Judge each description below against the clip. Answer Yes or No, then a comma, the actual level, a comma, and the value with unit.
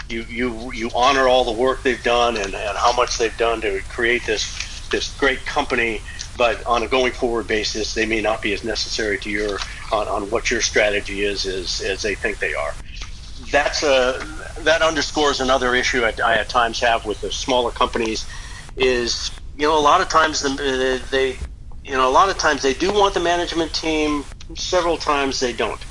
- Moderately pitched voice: No, low, 130 Hz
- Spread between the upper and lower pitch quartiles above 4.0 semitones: Yes, average, 4.5 semitones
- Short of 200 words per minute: No, fast, 205 wpm